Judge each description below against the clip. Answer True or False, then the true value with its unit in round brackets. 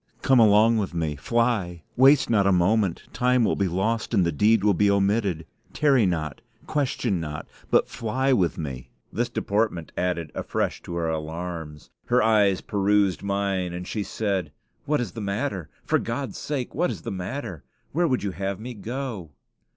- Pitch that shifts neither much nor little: True (4.9 semitones)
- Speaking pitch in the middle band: False (100 Hz)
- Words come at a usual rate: True (175 wpm)